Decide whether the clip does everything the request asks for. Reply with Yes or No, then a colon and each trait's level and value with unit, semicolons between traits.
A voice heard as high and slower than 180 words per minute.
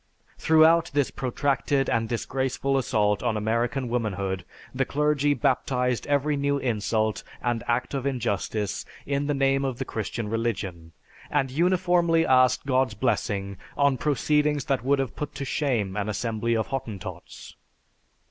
No: low, 130 Hz; average, 140 wpm